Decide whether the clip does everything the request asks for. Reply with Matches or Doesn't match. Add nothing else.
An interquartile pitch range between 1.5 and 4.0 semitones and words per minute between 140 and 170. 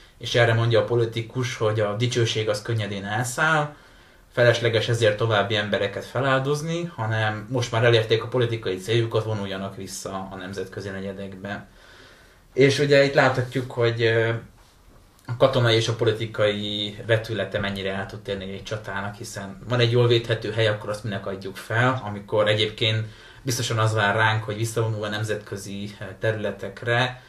Matches